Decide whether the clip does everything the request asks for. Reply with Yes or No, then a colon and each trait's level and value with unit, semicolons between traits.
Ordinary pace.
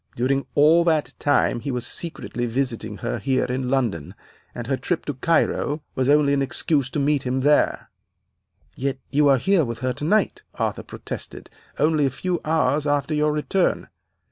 Yes: average, 170 wpm